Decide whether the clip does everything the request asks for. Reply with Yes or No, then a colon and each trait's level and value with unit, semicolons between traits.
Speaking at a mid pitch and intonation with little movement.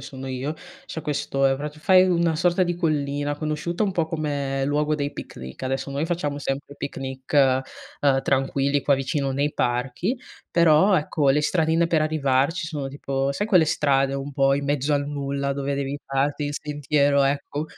Yes: medium, 145 Hz; narrow, 2.1 semitones